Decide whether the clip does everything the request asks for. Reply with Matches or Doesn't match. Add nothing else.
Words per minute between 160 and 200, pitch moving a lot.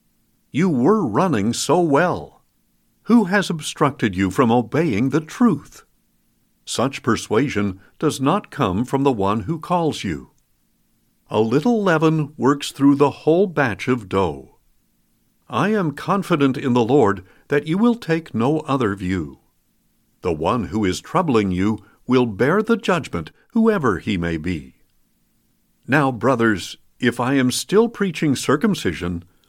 Doesn't match